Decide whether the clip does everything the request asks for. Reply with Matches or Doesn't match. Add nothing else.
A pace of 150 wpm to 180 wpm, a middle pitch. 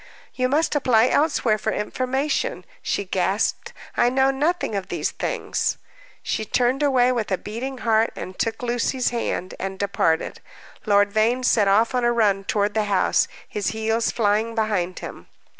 Doesn't match